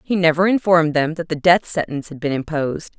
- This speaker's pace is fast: Yes, fast, 220 wpm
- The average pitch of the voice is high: No, medium, 165 Hz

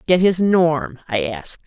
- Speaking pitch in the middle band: Yes, medium, 165 Hz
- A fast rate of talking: No, average, 180 wpm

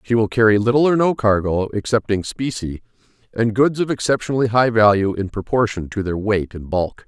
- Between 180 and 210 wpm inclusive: Yes, average, 185 wpm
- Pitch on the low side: Yes, low, 110 Hz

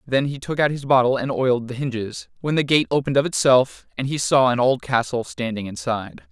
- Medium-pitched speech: No, low, 130 Hz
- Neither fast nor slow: No, fast, 230 wpm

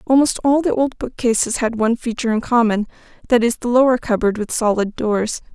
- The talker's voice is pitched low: No, high, 235 Hz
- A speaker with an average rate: Yes, average, 195 wpm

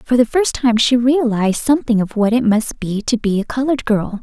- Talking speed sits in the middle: No, fast, 240 wpm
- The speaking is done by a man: No, female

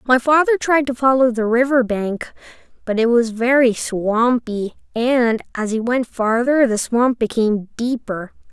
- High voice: Yes, high, 240 Hz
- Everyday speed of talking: Yes, average, 155 wpm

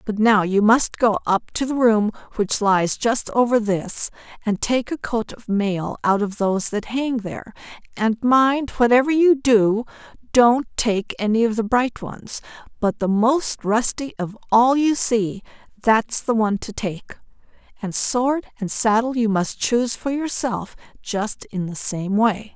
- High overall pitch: Yes, high, 225 Hz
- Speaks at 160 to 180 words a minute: Yes, average, 175 wpm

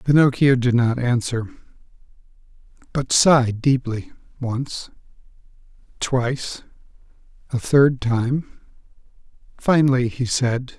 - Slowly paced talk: Yes, slow, 70 wpm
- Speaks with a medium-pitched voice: No, low, 125 Hz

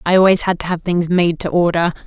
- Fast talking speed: Yes, fast, 260 wpm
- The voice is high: No, medium, 175 Hz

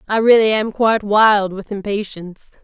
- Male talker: No, female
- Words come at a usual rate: Yes, average, 160 wpm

